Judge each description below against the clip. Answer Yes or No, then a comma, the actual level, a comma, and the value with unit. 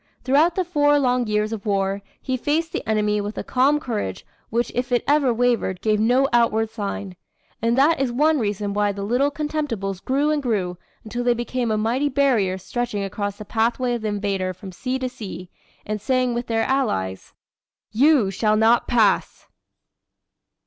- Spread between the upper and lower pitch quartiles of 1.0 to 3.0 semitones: No, average, 4.1 semitones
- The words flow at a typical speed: Yes, average, 180 wpm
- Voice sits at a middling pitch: No, high, 230 Hz